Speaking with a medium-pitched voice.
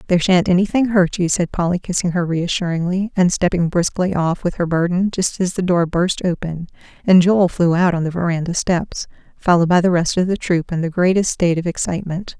Yes: medium, 175 Hz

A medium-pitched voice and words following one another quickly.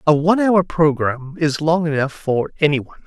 No: medium, 155 Hz; average, 195 wpm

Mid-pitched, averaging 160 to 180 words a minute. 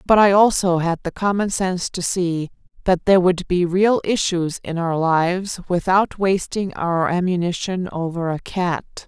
Yes: medium, 180 Hz; average, 165 wpm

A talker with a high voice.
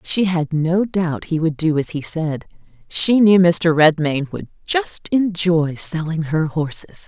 No: medium, 170 Hz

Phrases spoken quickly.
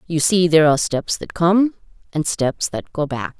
Yes: fast, 210 wpm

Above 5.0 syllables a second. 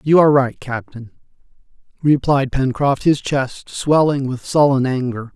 No: 4.4 syllables/s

